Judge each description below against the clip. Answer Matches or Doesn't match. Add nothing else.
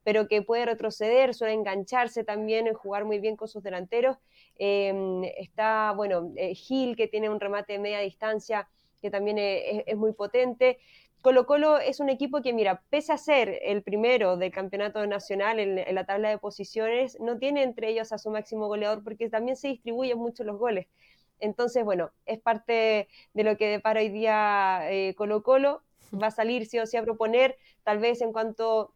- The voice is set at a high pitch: Matches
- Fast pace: Matches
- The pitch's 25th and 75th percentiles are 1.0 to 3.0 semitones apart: Matches